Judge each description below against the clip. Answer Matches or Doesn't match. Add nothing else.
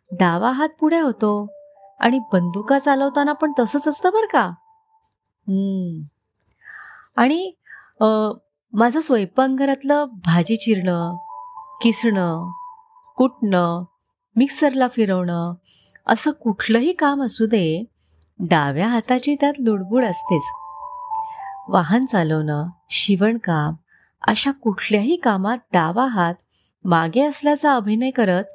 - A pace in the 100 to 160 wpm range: Doesn't match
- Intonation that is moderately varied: Doesn't match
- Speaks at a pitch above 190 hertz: Matches